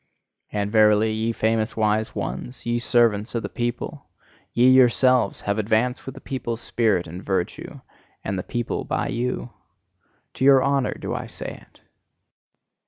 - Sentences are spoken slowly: No, average, 155 wpm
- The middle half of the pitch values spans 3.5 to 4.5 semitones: No, average, 2.7 semitones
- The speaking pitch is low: Yes, low, 115 Hz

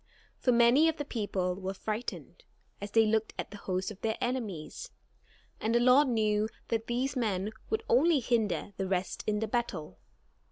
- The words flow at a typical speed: Yes, average, 175 wpm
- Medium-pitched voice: No, high, 220 Hz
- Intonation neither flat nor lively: Yes, average, 3.4 semitones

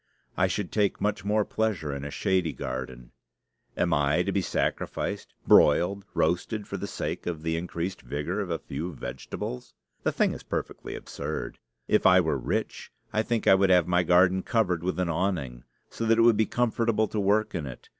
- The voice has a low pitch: Yes, very low, 90 Hz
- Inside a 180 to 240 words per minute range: Yes, average, 195 wpm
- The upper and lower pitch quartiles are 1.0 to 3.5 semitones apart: No, average, 4.7 semitones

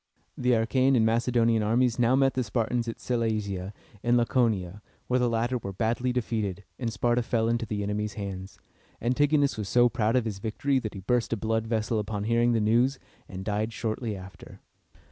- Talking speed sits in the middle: Yes, average, 190 wpm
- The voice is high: No, low, 115 Hz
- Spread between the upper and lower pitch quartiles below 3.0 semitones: Yes, narrow, 2.5 semitones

